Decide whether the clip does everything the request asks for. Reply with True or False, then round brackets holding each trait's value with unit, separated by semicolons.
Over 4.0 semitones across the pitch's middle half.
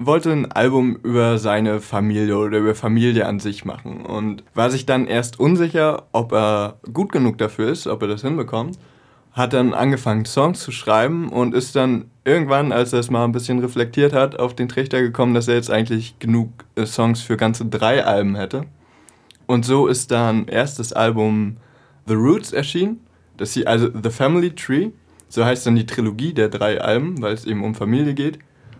False (3.2 semitones)